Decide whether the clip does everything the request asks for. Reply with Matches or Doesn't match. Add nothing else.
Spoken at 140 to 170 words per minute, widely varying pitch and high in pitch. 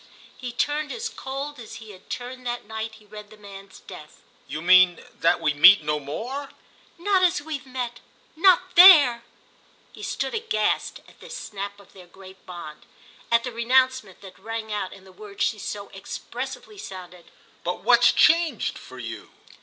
Matches